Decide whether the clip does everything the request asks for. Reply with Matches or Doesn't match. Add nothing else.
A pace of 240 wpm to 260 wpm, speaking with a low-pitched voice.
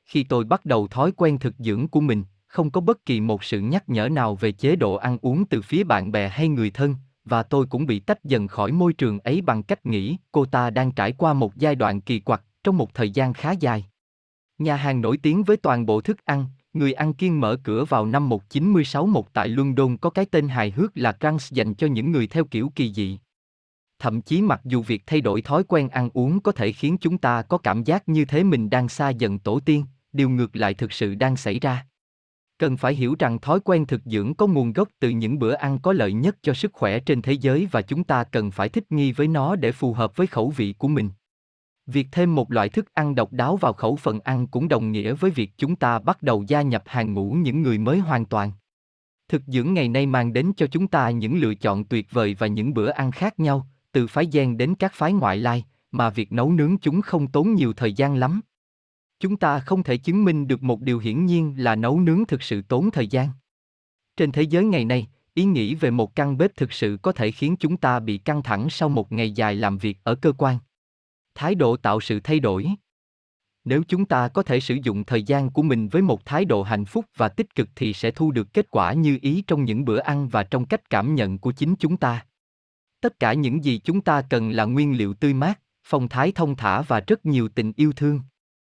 Matches